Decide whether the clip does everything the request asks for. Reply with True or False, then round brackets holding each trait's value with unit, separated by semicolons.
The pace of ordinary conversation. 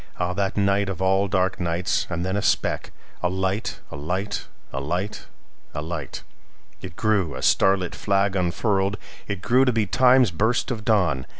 True (155 wpm)